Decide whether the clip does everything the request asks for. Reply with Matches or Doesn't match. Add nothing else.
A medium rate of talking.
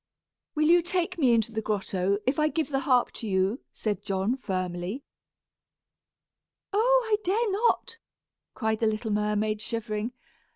Matches